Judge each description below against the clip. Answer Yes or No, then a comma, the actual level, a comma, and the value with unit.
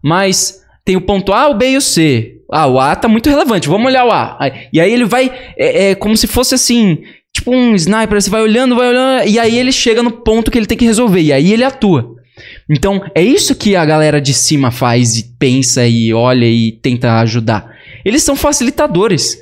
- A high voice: Yes, high, 205 Hz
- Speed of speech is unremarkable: No, fast, 220 wpm